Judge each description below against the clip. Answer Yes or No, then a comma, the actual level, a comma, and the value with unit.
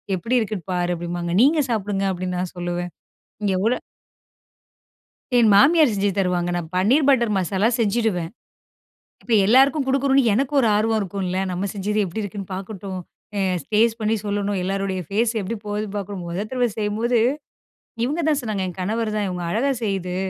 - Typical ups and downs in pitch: Yes, average, 3.8 semitones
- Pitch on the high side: Yes, high, 205 Hz